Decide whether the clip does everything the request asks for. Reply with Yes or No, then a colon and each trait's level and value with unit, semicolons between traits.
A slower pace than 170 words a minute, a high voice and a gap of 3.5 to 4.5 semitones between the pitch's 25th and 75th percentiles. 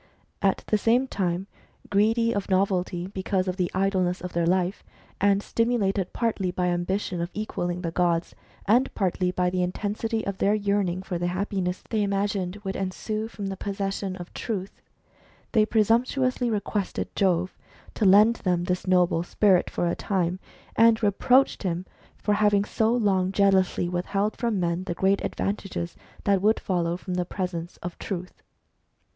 No: average, 160 wpm; high, 195 Hz; narrow, 2.5 semitones